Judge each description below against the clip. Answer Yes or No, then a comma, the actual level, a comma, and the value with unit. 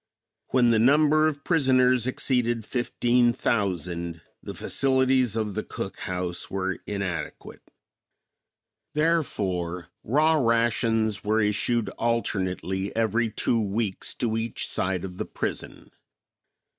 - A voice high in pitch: No, low, 115 Hz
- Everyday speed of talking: No, slow, 110 wpm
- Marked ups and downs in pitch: No, average, 4.5 semitones